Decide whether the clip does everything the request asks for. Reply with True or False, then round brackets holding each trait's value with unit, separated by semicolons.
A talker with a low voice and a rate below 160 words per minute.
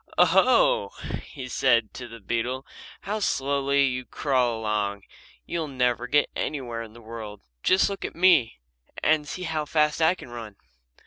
False (130 Hz; 165 wpm)